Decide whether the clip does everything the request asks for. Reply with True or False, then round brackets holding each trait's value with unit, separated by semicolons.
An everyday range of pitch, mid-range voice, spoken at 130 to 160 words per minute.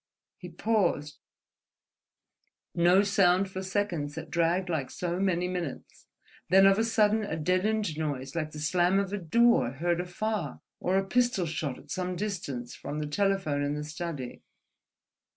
True (4.3 semitones; 180 Hz; 150 wpm)